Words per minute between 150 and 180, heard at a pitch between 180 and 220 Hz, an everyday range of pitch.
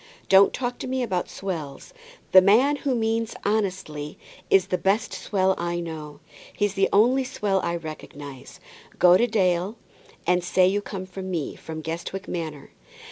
Yes: average, 165 wpm; high, 190 Hz; average, 3.7 semitones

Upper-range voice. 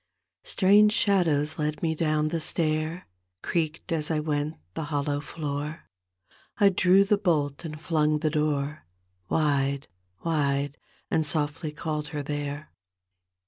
No: medium, 155 Hz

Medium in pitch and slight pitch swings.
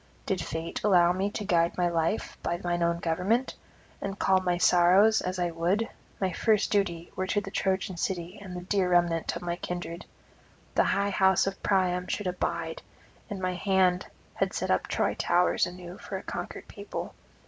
Yes: medium, 180 Hz; narrow, 1.9 semitones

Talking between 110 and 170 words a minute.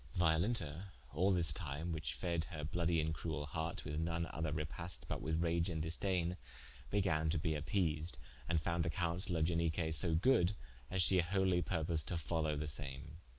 No: average, 180 wpm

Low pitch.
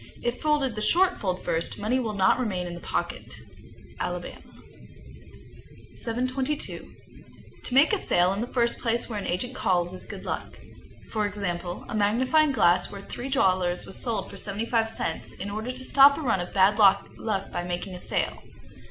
No: high, 215 Hz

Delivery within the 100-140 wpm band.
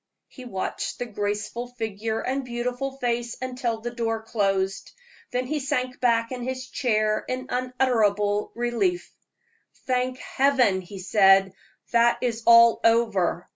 Yes: slow, 135 wpm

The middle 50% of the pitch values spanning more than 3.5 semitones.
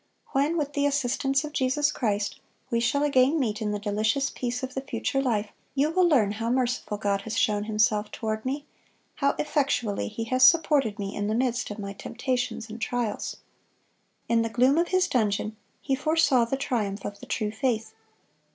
Yes: average, 4.3 semitones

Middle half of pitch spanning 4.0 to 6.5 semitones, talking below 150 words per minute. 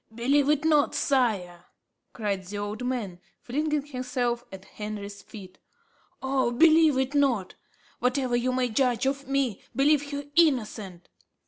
Yes: average, 4.9 semitones; slow, 135 wpm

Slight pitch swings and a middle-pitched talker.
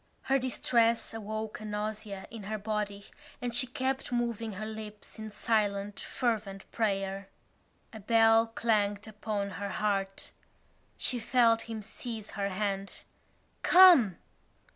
No: narrow, 2.2 semitones; high, 215 Hz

